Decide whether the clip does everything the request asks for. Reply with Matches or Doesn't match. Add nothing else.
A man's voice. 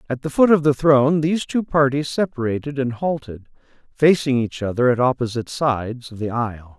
Matches